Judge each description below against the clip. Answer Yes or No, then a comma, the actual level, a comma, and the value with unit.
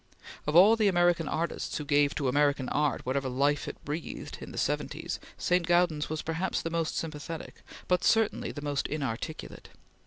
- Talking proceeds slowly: No, average, 175 wpm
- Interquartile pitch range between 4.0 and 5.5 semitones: No, average, 3.2 semitones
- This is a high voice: No, medium, 155 Hz